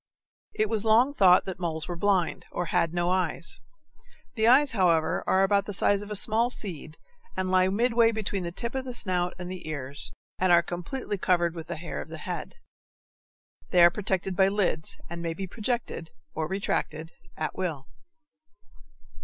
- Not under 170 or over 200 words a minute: Yes, average, 180 wpm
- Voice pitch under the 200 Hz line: Yes, medium, 185 Hz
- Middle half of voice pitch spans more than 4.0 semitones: No, average, 3.4 semitones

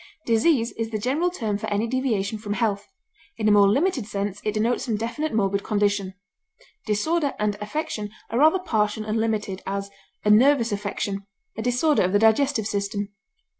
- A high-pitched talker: Yes, high, 215 Hz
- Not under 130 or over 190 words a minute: Yes, average, 170 wpm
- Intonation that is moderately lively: Yes, average, 3.2 semitones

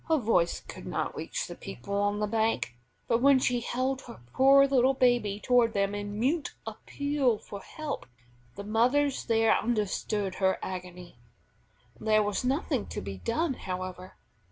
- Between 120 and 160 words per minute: Yes, average, 155 wpm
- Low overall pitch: No, high, 225 Hz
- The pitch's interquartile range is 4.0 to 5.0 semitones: Yes, average, 4.7 semitones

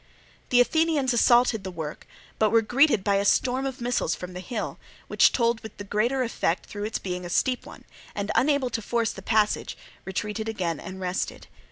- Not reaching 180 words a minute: No, average, 195 wpm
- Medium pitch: No, high, 220 Hz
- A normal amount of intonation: Yes, average, 4.4 semitones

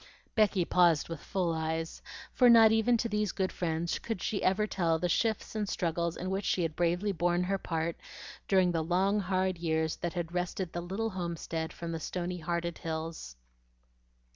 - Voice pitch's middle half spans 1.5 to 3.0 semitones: Yes, average, 2.7 semitones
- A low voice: No, medium, 175 Hz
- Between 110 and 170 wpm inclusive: No, average, 185 wpm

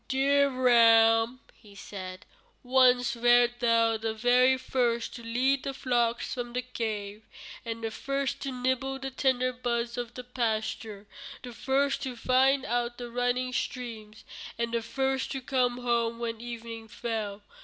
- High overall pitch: Yes, high, 245 Hz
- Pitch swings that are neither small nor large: No, narrow, 2.0 semitones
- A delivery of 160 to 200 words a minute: No, average, 150 wpm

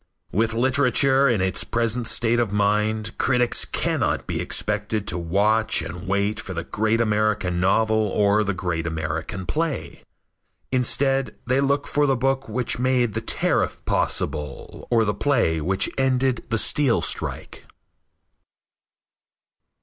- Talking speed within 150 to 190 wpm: No, slow, 135 wpm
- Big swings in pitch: No, average, 4.1 semitones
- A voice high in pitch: No, low, 110 Hz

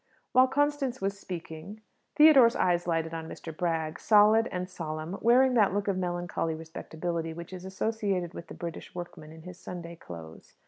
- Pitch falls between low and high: Yes, medium, 180 Hz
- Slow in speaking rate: No, average, 170 wpm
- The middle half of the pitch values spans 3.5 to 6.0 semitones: Yes, average, 4.3 semitones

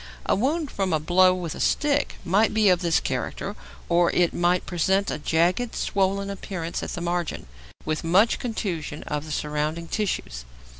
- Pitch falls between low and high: Yes, medium, 180 Hz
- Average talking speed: Yes, average, 170 wpm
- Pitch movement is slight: No, average, 3.3 semitones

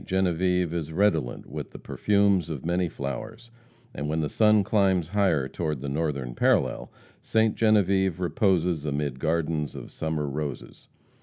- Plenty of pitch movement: No, average, 4.6 semitones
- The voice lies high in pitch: No, very low, 85 Hz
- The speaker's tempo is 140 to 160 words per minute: Yes, average, 145 wpm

